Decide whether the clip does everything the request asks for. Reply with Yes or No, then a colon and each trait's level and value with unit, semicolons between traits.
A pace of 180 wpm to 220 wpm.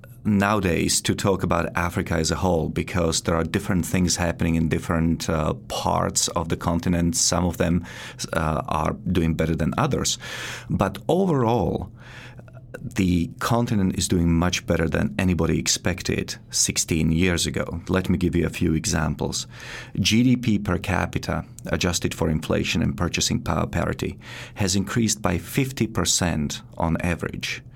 No: average, 145 wpm